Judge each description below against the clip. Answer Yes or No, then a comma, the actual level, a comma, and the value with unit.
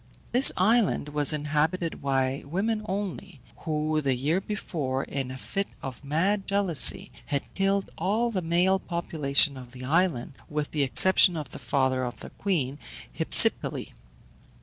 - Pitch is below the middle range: No, medium, 155 Hz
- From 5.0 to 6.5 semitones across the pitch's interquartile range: Yes, wide, 5.6 semitones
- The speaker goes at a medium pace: Yes, average, 150 wpm